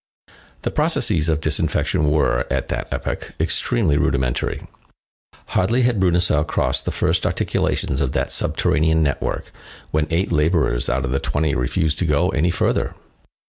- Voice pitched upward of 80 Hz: No, very low, 75 Hz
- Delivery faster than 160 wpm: No, average, 145 wpm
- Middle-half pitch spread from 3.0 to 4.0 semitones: Yes, average, 3.3 semitones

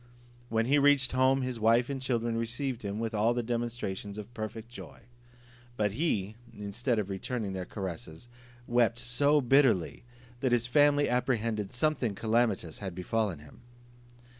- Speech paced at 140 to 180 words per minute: Yes, average, 150 wpm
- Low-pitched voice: Yes, low, 115 Hz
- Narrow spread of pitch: No, average, 3.2 semitones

